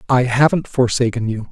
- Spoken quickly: No, average, 160 wpm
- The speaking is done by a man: Yes, male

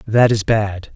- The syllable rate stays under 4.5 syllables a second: Yes, 3.7 syllables/s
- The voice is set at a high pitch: No, low, 105 Hz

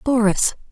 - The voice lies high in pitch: Yes, high, 225 Hz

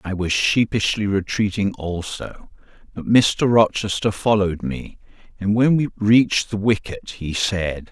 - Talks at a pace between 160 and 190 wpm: No, slow, 135 wpm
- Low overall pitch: Yes, low, 100 Hz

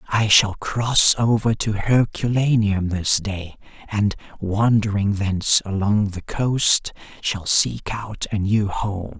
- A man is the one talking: Yes, male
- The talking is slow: Yes, slow, 130 wpm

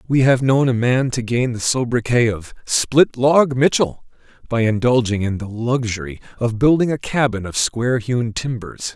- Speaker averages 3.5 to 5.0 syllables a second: Yes, 4.6 syllables/s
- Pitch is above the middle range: No, low, 120 Hz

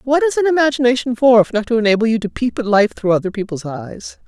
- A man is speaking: No, female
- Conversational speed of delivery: No, fast, 255 wpm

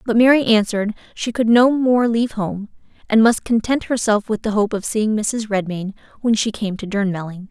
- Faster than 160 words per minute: Yes, average, 200 wpm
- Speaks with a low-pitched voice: No, high, 220 Hz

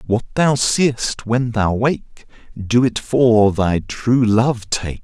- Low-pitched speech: Yes, low, 115 Hz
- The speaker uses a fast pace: No, average, 155 wpm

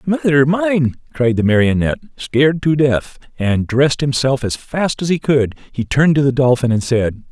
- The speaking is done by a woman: No, male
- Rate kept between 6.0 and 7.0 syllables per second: No, 5.0 syllables/s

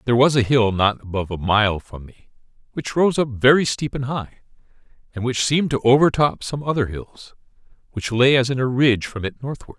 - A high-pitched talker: No, low, 120 Hz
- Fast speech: Yes, fast, 210 wpm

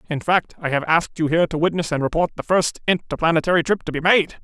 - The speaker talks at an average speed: No, fast, 245 wpm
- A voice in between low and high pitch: Yes, medium, 165 Hz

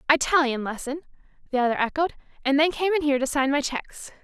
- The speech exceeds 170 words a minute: Yes, average, 200 wpm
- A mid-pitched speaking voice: No, very high, 285 Hz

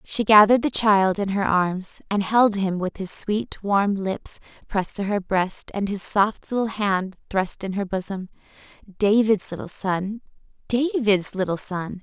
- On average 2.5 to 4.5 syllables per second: Yes, 4.1 syllables/s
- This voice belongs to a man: No, female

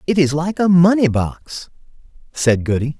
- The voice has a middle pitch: Yes, medium, 160 Hz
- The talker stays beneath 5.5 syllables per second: Yes, 4.5 syllables/s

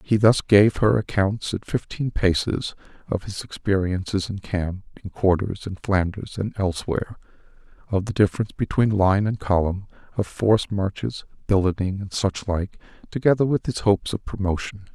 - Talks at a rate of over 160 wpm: No, average, 155 wpm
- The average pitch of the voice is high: No, low, 100 Hz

